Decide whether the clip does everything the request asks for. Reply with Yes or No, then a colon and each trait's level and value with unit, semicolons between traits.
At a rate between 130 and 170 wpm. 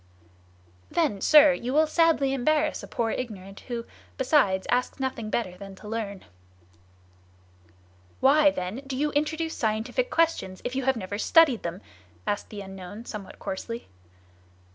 Yes: average, 140 wpm